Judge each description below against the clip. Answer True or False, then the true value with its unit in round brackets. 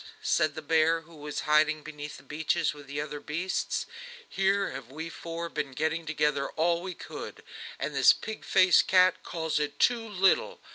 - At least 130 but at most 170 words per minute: False (180 wpm)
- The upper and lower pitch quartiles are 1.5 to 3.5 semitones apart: True (2.4 semitones)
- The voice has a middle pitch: True (160 Hz)